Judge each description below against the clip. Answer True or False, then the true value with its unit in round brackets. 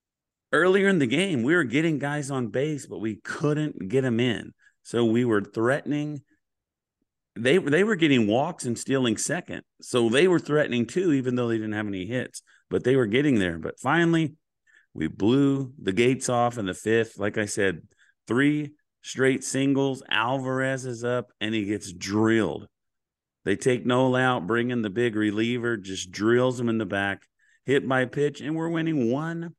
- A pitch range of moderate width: True (3.9 semitones)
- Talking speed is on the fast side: False (185 wpm)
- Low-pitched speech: True (125 Hz)